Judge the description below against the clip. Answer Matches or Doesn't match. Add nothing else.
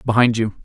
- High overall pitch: Doesn't match